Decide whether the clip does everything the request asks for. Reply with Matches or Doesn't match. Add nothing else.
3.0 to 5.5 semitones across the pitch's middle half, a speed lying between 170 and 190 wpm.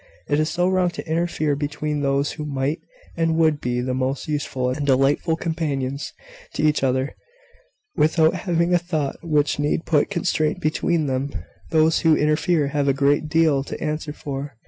Doesn't match